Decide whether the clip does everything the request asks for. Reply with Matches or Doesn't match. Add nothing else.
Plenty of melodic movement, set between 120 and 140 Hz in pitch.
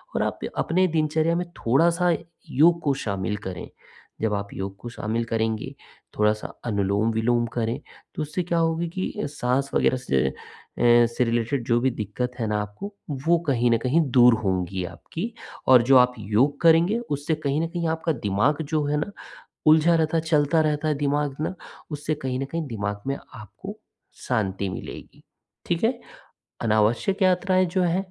Matches